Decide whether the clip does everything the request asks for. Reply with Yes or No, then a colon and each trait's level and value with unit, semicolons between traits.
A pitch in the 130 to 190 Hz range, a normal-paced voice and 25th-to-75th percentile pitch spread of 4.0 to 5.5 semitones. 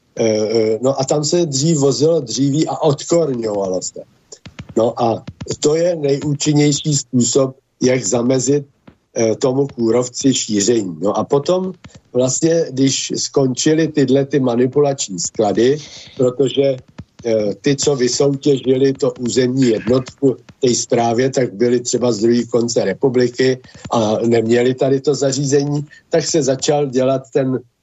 No: low, 135 Hz; average, 125 wpm; average, 2.8 semitones